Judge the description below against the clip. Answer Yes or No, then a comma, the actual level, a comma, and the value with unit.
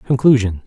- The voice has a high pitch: No, low, 115 Hz